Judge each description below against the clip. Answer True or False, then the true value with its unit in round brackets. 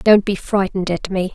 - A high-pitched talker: True (195 Hz)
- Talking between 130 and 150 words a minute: False (225 wpm)